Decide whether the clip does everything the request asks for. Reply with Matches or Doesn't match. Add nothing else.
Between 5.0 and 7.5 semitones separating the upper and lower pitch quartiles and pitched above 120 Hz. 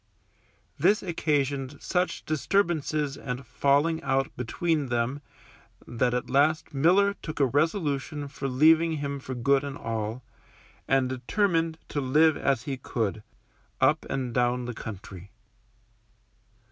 Doesn't match